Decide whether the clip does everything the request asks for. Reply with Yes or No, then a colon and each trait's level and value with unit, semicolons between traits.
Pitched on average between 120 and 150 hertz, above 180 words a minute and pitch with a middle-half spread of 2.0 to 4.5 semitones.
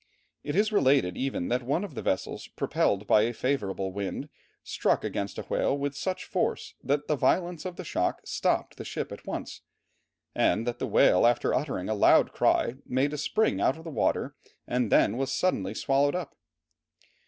No: low, 135 Hz; average, 190 wpm; wide, 5.6 semitones